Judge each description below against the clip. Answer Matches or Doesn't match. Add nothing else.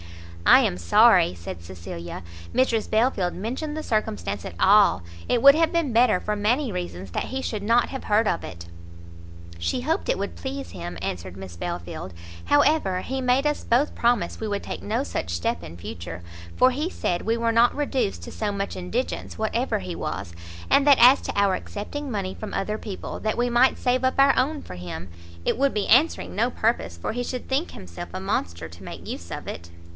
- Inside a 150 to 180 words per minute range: Doesn't match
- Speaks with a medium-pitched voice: Doesn't match